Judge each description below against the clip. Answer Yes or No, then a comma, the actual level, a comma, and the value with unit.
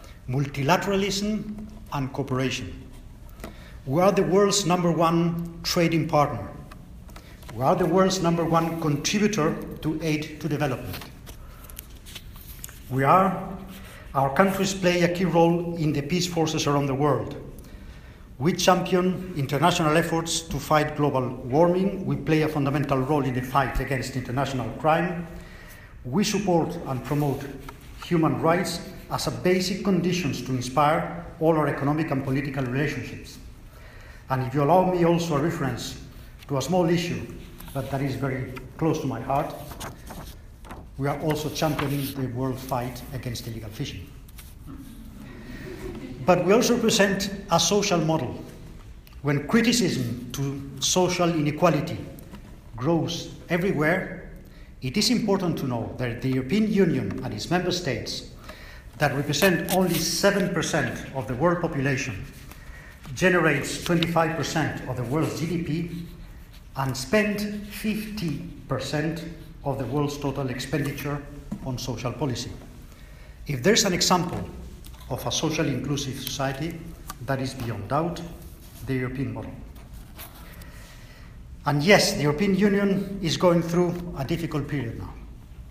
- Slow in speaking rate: Yes, slow, 130 wpm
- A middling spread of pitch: Yes, average, 4.8 semitones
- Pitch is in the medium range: Yes, medium, 150 Hz